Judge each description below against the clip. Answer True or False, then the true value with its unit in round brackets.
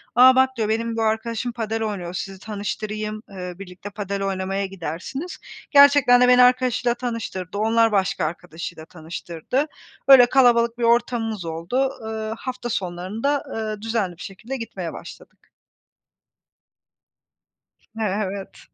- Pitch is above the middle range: True (220 Hz)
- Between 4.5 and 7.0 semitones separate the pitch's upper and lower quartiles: False (4.1 semitones)